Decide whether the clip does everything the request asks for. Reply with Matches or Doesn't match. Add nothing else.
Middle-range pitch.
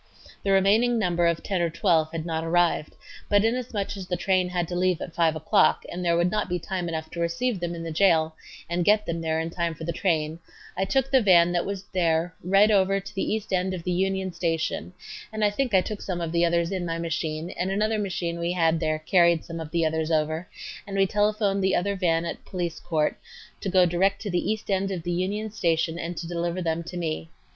Matches